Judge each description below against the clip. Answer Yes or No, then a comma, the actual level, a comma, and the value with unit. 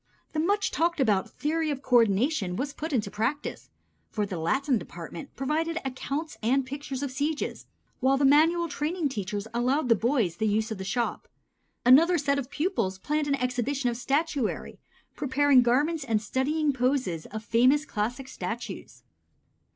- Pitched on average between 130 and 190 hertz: No, very high, 265 Hz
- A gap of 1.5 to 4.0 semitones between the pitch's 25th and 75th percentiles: No, average, 4.5 semitones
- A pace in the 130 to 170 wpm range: Yes, average, 160 wpm